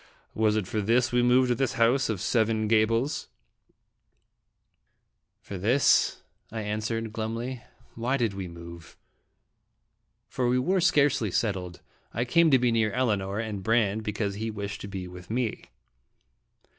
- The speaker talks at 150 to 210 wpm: Yes, average, 155 wpm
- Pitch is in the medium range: No, low, 110 Hz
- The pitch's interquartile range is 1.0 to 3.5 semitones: Yes, average, 3.2 semitones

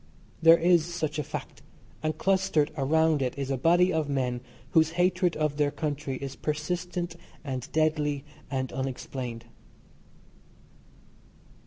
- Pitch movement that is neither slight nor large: Yes, average, 3.4 semitones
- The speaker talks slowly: Yes, slow, 130 wpm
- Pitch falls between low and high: Yes, medium, 155 Hz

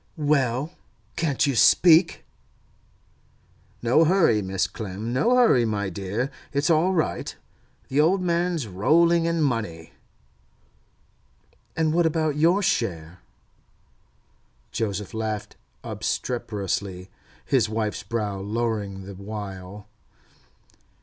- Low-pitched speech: Yes, low, 115 Hz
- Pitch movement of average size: No, wide, 7.8 semitones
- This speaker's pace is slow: Yes, slow, 100 wpm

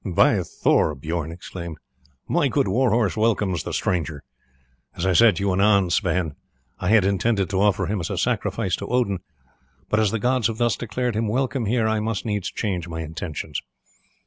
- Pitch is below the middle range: Yes, low, 100 Hz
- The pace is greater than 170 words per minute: Yes, average, 190 wpm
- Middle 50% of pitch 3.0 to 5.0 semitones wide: Yes, average, 4.0 semitones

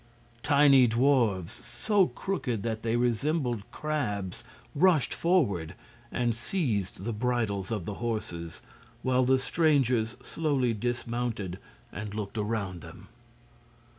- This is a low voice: Yes, low, 120 Hz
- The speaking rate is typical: No, slow, 110 wpm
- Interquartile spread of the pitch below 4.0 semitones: No, average, 4.5 semitones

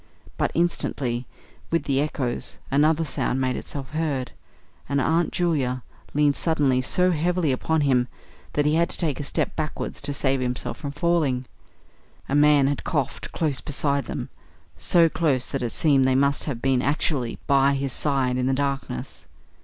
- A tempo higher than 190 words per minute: No, average, 170 wpm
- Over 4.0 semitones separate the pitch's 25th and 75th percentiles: No, average, 2.8 semitones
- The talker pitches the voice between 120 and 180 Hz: Yes, medium, 140 Hz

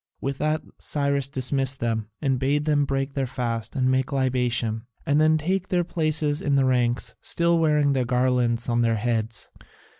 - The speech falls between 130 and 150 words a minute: No, average, 175 wpm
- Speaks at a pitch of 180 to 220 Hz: No, low, 135 Hz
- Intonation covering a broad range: No, average, 3.4 semitones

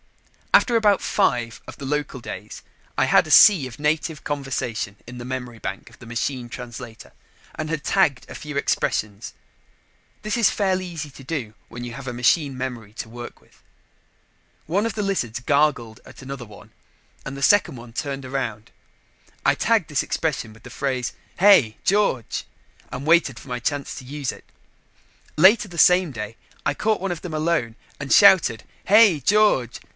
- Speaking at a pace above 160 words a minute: Yes, average, 175 wpm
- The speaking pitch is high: No, low, 135 Hz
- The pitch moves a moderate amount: No, wide, 5.9 semitones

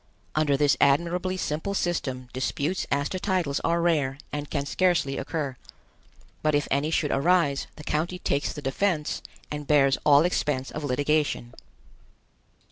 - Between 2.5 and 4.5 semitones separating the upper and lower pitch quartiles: Yes, average, 3.3 semitones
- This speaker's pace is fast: No, average, 145 wpm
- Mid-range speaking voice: Yes, medium, 150 Hz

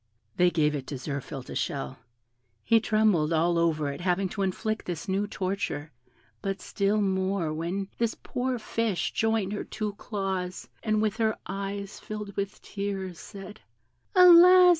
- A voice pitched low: No, high, 195 Hz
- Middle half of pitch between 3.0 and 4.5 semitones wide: Yes, average, 3.6 semitones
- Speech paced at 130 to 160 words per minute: Yes, average, 155 wpm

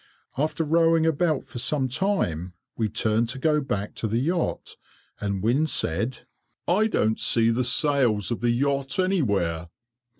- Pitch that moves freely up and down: Yes, wide, 6.1 semitones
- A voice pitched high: No, low, 130 Hz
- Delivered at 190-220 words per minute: No, average, 155 wpm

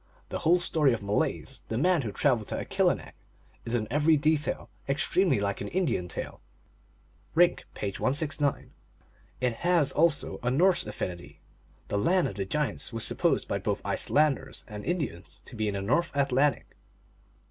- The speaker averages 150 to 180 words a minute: Yes, average, 165 wpm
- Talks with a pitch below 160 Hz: Yes, medium, 140 Hz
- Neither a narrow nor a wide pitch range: No, wide, 6.8 semitones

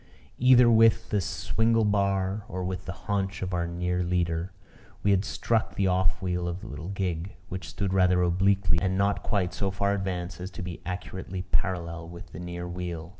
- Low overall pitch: Yes, very low, 95 Hz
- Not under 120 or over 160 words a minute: No, average, 190 wpm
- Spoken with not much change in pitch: Yes, narrow, 2.0 semitones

